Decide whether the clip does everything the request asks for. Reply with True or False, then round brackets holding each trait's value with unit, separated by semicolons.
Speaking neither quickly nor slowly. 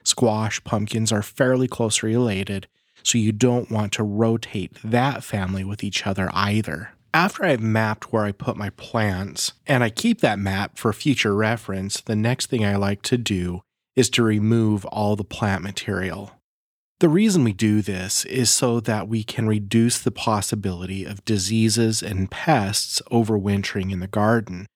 True (165 wpm)